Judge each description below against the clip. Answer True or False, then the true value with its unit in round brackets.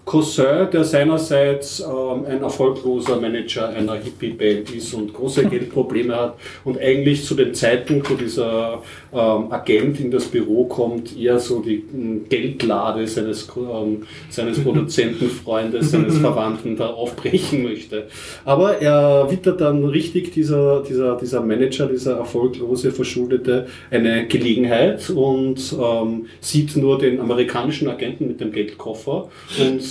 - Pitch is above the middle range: False (130 Hz)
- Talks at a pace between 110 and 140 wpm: True (130 wpm)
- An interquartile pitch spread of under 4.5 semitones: True (3.5 semitones)